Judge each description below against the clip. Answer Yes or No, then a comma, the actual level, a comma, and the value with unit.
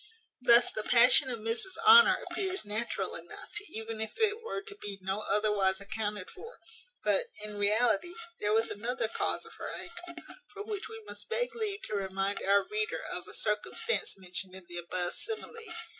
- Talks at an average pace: Yes, average, 175 wpm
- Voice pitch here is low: No, high, 230 Hz